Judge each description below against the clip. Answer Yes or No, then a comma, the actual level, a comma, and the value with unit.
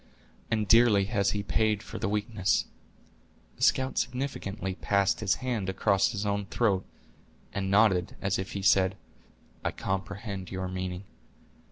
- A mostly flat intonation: Yes, narrow, 2.1 semitones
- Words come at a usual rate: Yes, average, 145 wpm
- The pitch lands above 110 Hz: No, low, 100 Hz